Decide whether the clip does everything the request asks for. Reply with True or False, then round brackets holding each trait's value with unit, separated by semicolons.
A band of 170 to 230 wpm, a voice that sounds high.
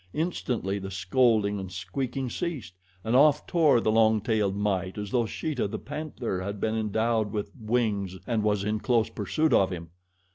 False (175 wpm; 110 Hz)